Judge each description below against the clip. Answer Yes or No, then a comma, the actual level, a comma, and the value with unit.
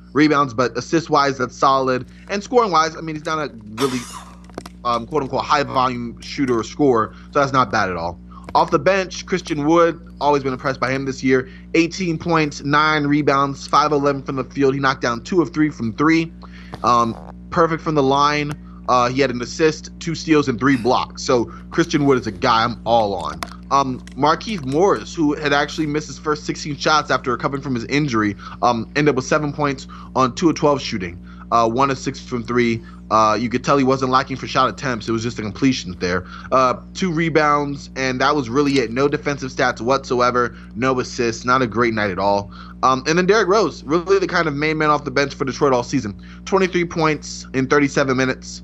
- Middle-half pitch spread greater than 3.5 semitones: Yes, average, 4.1 semitones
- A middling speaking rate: No, fast, 215 wpm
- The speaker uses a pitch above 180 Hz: No, low, 135 Hz